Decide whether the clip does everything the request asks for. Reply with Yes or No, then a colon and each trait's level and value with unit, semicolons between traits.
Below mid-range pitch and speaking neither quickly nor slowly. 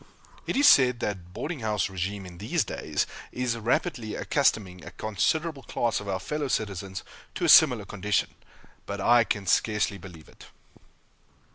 Yes: low, 105 Hz; average, 155 wpm